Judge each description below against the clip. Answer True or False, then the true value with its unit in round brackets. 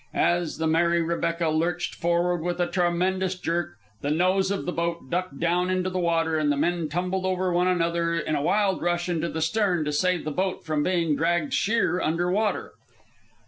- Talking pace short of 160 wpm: False (195 wpm)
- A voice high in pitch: False (175 Hz)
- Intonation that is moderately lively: False (1.9 semitones)